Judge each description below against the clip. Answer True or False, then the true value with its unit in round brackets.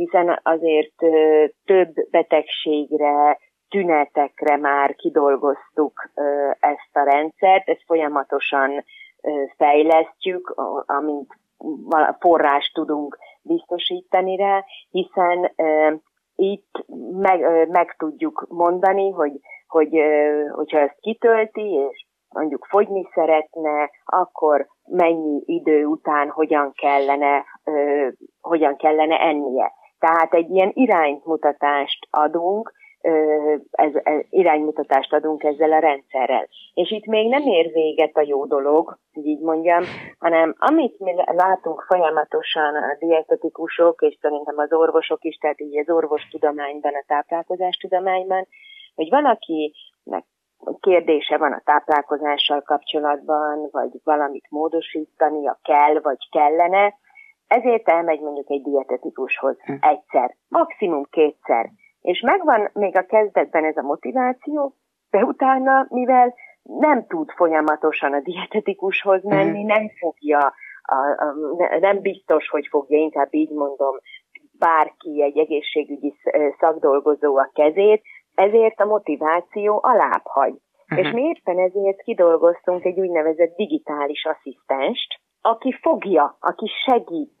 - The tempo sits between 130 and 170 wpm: False (105 wpm)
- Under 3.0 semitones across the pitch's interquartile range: False (4.2 semitones)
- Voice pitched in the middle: True (160 Hz)